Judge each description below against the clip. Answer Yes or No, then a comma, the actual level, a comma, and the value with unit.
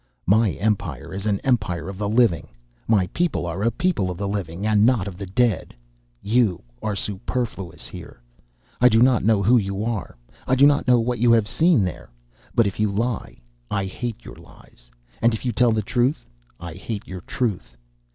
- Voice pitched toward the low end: Yes, low, 105 Hz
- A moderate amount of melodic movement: Yes, average, 3.9 semitones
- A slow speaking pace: No, average, 195 wpm